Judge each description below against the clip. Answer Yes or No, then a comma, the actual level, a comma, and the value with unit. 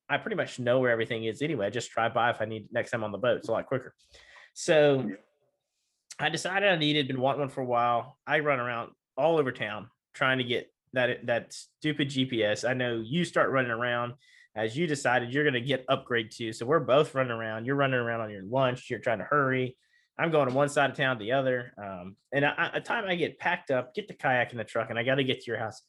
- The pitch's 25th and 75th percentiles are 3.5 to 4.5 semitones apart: Yes, average, 3.9 semitones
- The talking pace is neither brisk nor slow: No, fast, 255 wpm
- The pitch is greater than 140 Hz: No, low, 130 Hz